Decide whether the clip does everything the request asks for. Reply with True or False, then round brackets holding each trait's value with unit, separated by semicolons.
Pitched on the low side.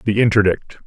True (105 Hz)